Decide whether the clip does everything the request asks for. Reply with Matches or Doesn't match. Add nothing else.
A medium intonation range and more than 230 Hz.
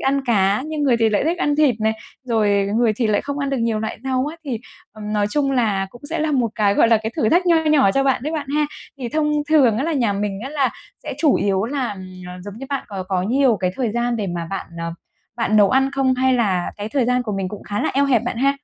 Matches